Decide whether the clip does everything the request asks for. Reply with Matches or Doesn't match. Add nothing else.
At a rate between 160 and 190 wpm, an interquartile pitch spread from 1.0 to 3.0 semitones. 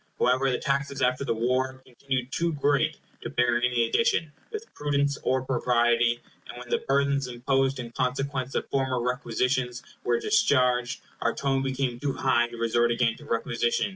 Matches